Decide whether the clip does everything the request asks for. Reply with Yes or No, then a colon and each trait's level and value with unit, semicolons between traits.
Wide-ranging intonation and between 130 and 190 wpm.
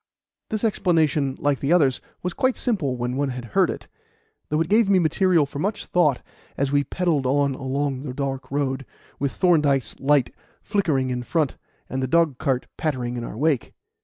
No: average, 4.2 semitones; average, 180 wpm